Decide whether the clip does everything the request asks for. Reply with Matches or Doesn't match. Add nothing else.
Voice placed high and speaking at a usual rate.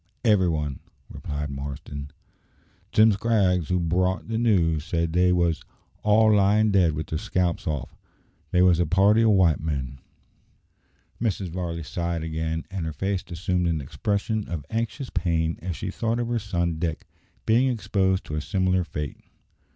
Doesn't match